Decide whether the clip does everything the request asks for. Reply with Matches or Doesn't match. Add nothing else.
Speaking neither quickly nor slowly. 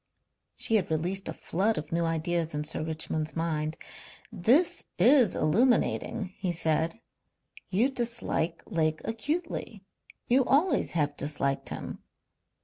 Doesn't match